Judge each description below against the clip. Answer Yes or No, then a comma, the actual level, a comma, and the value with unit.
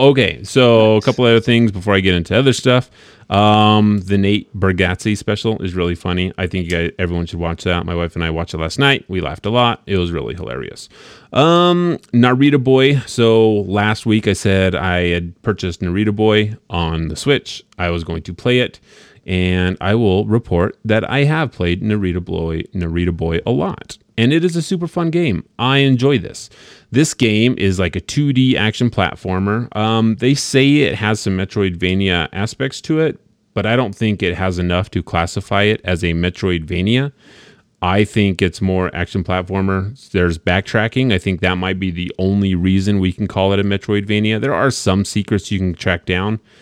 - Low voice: Yes, low, 100 Hz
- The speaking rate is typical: Yes, average, 195 wpm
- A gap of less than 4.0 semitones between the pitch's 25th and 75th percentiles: No, average, 4.4 semitones